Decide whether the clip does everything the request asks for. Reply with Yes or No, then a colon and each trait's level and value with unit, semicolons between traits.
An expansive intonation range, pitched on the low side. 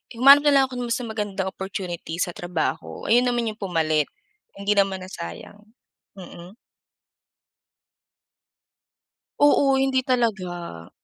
No: wide, 5.7 semitones; high, 200 Hz